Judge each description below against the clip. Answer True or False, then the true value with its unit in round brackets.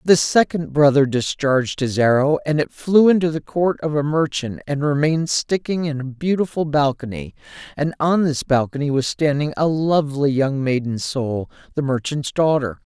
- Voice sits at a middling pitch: True (145 Hz)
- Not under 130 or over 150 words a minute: False (165 wpm)